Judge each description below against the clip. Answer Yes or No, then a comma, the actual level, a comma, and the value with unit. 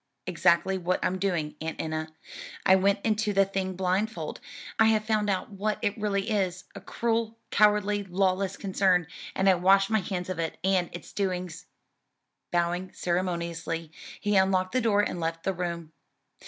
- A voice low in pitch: No, high, 190 Hz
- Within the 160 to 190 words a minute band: Yes, average, 165 wpm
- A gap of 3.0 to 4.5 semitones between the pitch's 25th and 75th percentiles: No, narrow, 2.5 semitones